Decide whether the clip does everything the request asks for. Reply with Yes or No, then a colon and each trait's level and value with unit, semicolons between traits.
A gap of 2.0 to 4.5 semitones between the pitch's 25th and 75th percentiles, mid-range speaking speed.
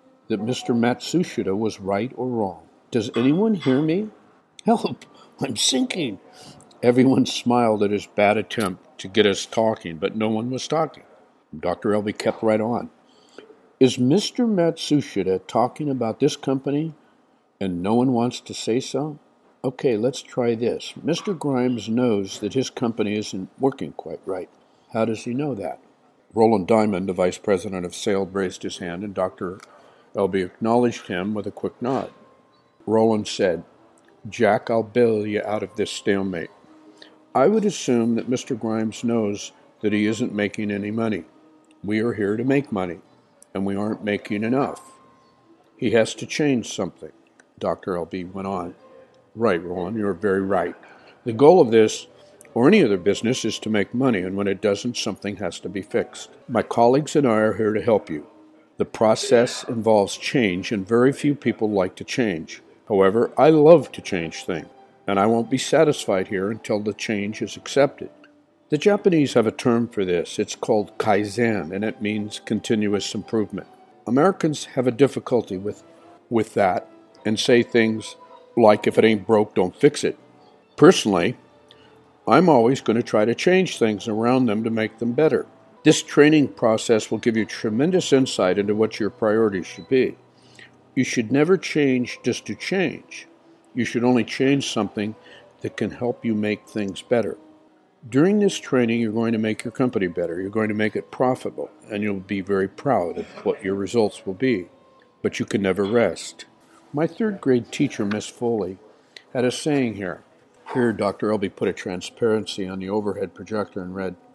Yes: average, 3.8 semitones; average, 170 wpm